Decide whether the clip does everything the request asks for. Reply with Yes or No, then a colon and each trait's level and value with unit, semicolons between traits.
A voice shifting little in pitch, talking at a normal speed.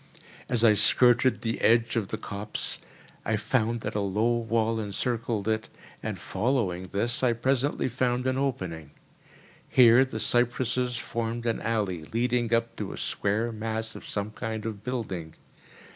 Yes: narrow, 2.3 semitones; average, 155 wpm